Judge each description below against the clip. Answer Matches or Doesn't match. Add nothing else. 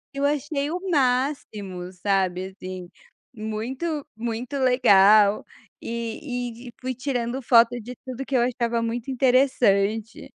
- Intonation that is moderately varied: Matches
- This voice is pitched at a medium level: Doesn't match